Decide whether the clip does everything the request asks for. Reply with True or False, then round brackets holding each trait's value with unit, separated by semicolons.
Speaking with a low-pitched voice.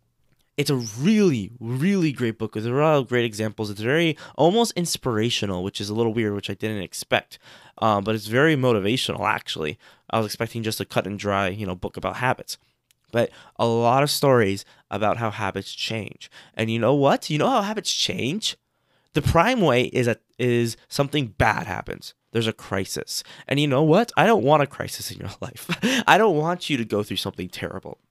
True (120 Hz)